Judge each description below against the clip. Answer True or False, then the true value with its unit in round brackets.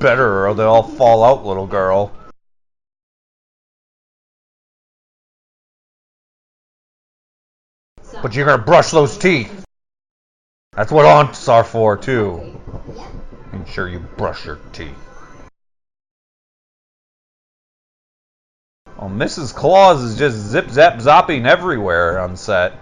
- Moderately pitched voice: False (105 Hz)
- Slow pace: True (95 wpm)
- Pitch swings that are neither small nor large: True (3.8 semitones)